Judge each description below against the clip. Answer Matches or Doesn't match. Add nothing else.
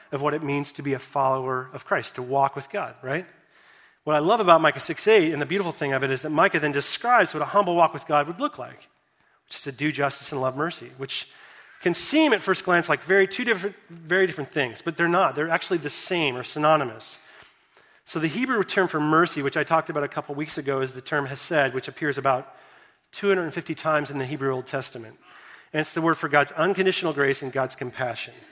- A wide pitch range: Doesn't match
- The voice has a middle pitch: Matches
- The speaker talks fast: Matches